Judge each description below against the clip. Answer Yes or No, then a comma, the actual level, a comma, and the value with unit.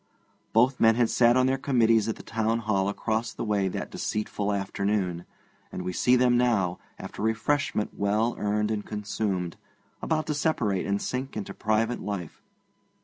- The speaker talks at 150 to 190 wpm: Yes, average, 165 wpm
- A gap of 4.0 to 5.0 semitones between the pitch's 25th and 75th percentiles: No, average, 3.1 semitones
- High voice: No, low, 110 Hz